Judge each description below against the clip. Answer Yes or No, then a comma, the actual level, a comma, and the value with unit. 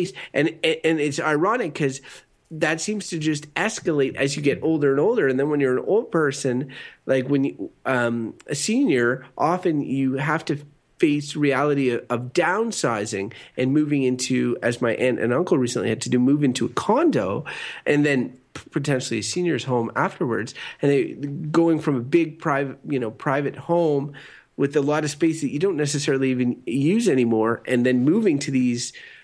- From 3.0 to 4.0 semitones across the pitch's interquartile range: Yes, average, 3.3 semitones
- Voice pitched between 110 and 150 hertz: Yes, medium, 140 Hz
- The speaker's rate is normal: Yes, average, 185 wpm